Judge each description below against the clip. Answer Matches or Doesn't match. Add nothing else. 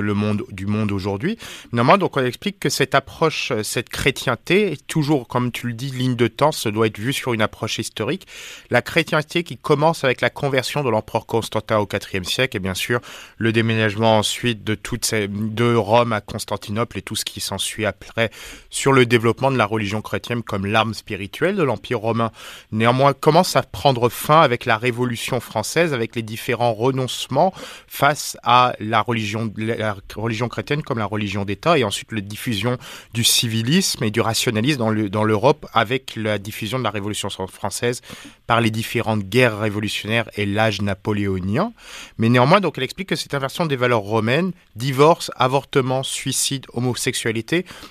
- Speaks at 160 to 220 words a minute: Matches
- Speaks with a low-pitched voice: Matches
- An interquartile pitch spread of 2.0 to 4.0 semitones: Matches